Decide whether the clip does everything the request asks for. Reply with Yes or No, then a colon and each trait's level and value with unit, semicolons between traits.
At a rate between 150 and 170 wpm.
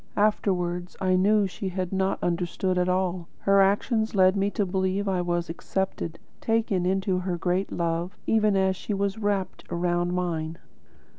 Yes: average, 165 wpm